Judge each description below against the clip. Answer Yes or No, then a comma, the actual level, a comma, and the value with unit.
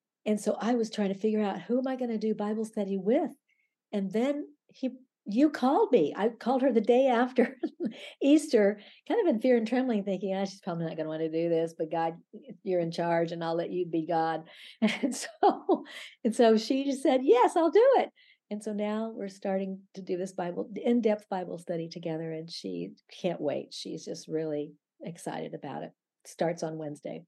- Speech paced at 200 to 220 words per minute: Yes, fast, 205 wpm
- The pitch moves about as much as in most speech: No, wide, 6.8 semitones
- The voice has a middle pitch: No, high, 210 Hz